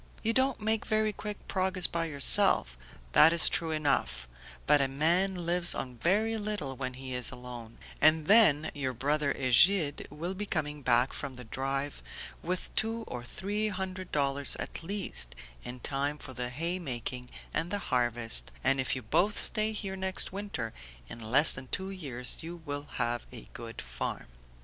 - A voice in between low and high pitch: Yes, medium, 150 Hz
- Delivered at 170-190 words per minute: Yes, average, 175 wpm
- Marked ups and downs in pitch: Yes, wide, 6.9 semitones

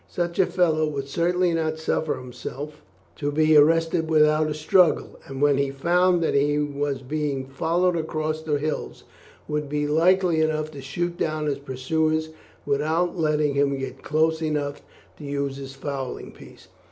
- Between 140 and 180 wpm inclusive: Yes, average, 165 wpm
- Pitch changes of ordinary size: No, narrow, 2.2 semitones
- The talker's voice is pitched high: No, medium, 155 Hz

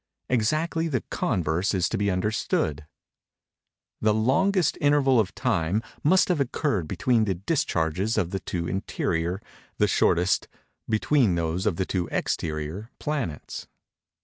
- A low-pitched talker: Yes, low, 105 Hz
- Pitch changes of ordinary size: No, wide, 7.5 semitones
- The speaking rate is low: Yes, slow, 130 wpm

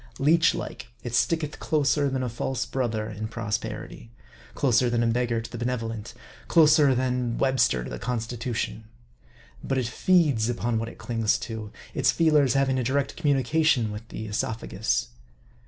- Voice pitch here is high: No, low, 120 Hz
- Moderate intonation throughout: Yes, average, 3.2 semitones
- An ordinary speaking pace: Yes, average, 160 wpm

